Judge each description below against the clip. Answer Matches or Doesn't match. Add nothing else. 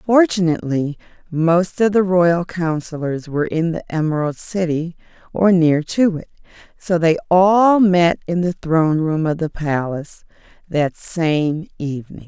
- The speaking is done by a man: Doesn't match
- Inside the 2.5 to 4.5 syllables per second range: Matches